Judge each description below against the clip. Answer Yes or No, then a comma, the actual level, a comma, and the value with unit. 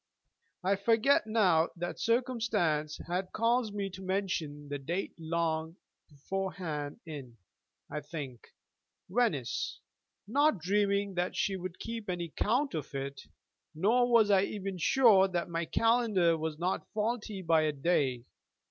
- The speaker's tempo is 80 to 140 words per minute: Yes, slow, 135 wpm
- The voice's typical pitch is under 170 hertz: No, medium, 185 Hz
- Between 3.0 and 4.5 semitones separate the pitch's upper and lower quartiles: No, average, 5.1 semitones